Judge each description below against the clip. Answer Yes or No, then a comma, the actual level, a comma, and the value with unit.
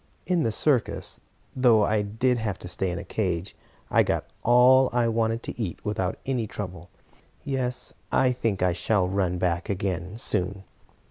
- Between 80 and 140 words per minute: No, average, 165 wpm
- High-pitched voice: No, low, 105 Hz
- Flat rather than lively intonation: No, average, 4.9 semitones